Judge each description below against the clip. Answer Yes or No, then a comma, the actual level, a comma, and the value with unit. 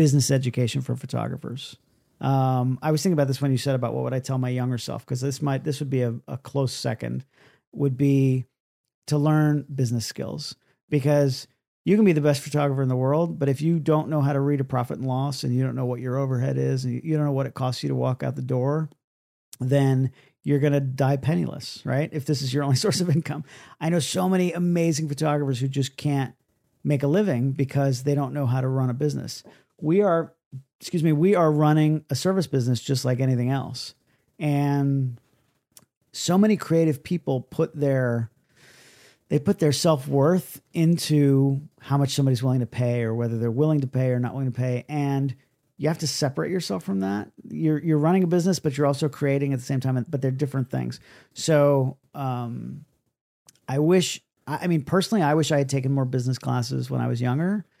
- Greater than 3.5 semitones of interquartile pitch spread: No, average, 2.9 semitones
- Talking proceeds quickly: Yes, fast, 210 wpm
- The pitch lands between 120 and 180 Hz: Yes, medium, 140 Hz